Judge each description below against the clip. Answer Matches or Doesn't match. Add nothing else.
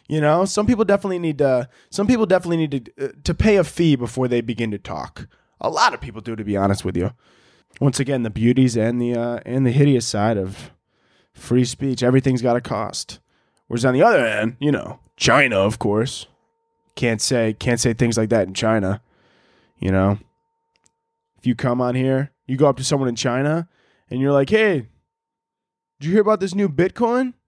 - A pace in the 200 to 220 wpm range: Matches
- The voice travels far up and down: Matches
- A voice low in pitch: Matches